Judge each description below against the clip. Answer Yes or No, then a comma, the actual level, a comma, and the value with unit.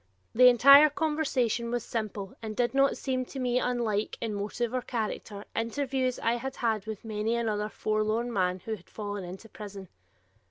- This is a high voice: Yes, high, 230 Hz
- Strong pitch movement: No, average, 3.0 semitones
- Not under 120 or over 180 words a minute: Yes, average, 170 wpm